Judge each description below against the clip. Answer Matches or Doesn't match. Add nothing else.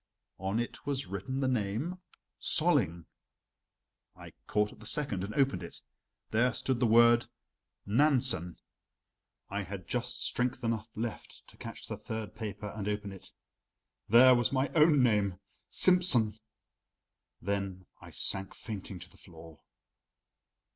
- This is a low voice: Matches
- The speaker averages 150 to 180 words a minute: Doesn't match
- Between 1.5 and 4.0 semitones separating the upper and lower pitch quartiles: Doesn't match